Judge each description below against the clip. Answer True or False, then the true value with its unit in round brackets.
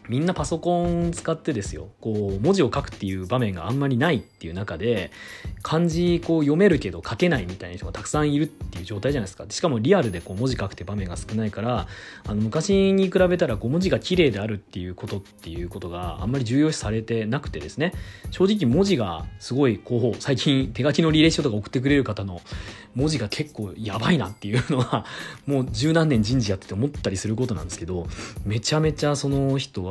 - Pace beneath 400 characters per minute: False (460 characters per minute)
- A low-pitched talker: True (120 Hz)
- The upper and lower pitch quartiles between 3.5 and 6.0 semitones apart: False (7.1 semitones)